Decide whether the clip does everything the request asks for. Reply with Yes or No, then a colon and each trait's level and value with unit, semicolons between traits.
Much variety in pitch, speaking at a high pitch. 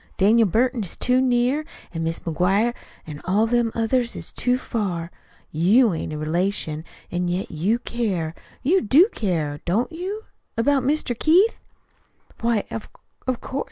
Yes: wide, 6.3 semitones; high, 225 Hz